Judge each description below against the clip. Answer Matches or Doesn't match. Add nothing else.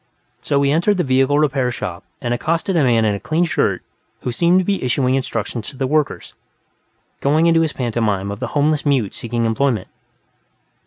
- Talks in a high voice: Doesn't match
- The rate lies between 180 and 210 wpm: Matches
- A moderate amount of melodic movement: Matches